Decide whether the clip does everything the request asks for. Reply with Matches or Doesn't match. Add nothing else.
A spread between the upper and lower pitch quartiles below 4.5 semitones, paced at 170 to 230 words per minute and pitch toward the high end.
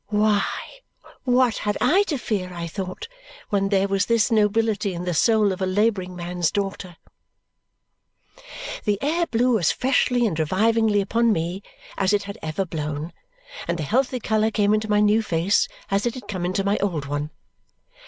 Matches